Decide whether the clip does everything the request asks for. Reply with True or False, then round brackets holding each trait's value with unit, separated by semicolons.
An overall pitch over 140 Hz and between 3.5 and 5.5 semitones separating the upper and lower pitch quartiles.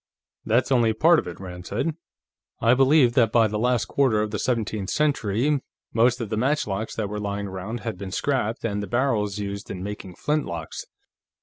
False (110 Hz; 3.8 semitones)